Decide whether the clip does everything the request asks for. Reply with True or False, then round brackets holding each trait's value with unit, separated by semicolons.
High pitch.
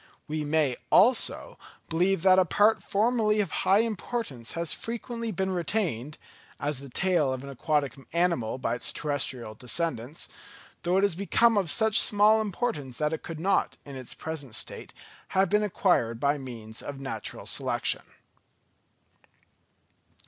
False (165 Hz)